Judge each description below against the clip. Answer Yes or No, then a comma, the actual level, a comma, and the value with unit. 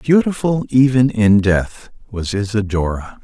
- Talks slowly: Yes, slow, 110 wpm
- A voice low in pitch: Yes, low, 110 Hz